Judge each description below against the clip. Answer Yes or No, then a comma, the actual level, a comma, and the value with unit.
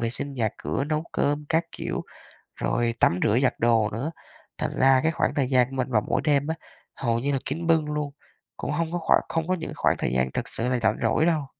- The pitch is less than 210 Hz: Yes, medium, 140 Hz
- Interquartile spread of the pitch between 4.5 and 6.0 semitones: Yes, average, 4.8 semitones